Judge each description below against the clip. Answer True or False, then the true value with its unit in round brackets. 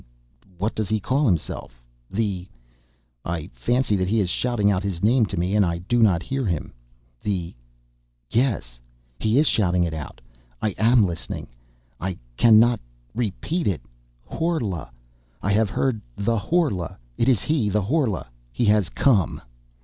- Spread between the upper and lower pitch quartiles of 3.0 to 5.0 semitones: True (4.7 semitones)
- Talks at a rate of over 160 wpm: False (155 wpm)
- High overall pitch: False (105 Hz)